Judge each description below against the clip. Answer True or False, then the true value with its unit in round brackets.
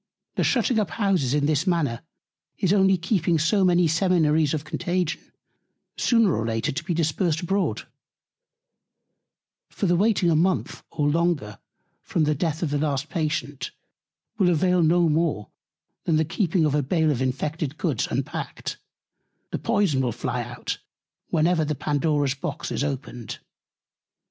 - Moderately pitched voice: True (160 Hz)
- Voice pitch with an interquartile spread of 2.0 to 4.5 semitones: True (3.6 semitones)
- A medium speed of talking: True (145 wpm)